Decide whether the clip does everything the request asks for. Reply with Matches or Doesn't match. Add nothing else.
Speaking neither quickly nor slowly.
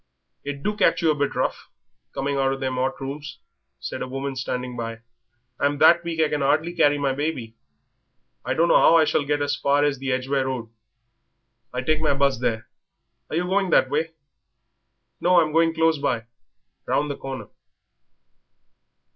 Matches